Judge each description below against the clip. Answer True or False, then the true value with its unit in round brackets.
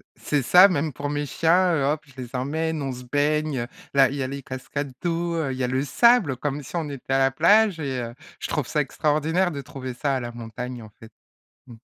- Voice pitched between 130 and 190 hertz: True (140 Hz)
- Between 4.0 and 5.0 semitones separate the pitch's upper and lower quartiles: False (3.5 semitones)